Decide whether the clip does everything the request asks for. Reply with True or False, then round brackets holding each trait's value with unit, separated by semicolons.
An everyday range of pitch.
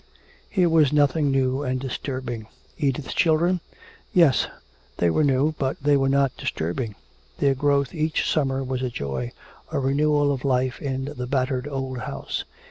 False (2.2 semitones)